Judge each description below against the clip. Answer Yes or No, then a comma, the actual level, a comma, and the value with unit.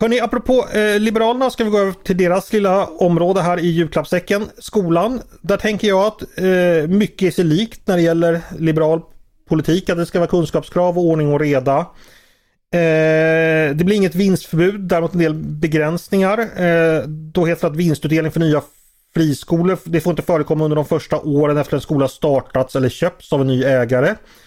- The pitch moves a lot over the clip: No, average, 3.3 semitones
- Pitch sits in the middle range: Yes, medium, 170 Hz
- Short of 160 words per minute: No, average, 190 wpm